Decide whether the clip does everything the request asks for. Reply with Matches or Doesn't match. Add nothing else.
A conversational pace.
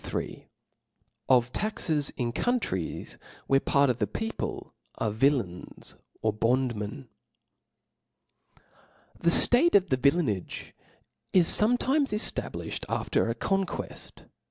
Doesn't match